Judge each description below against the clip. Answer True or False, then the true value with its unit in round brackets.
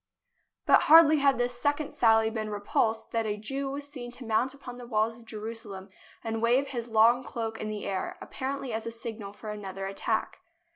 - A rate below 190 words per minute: False (205 wpm)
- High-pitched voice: True (230 Hz)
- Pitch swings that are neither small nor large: True (3.0 semitones)